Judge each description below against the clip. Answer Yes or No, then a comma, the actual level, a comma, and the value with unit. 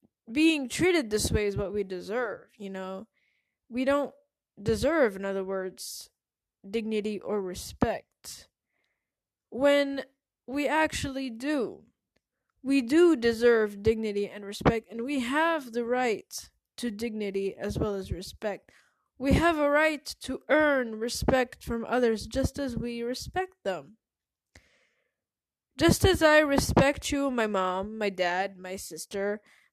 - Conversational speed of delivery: No, slow, 130 wpm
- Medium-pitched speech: No, high, 240 Hz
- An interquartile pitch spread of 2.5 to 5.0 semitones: No, wide, 5.5 semitones